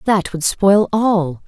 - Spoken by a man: No, female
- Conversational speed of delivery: Yes, average, 165 wpm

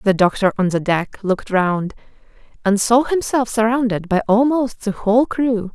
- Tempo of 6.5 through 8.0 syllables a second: No, 4.8 syllables/s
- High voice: Yes, high, 220 Hz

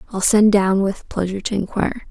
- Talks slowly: No, average, 200 wpm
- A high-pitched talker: Yes, high, 200 Hz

